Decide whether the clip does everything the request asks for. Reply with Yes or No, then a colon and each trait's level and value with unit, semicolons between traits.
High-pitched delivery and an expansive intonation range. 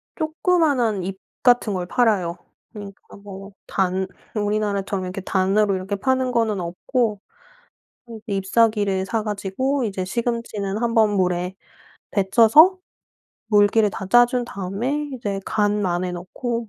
No: high, 205 Hz; average, 3.6 semitones